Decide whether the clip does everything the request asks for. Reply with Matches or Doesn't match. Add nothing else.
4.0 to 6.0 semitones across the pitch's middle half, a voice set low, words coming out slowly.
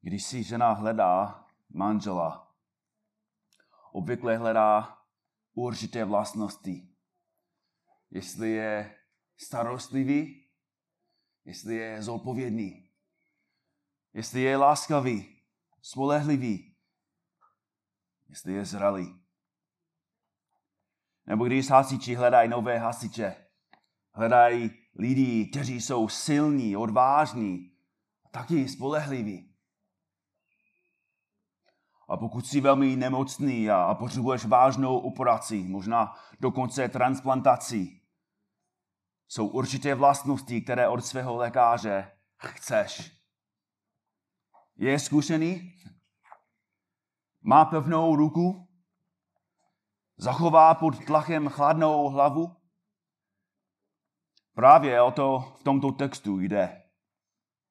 Matches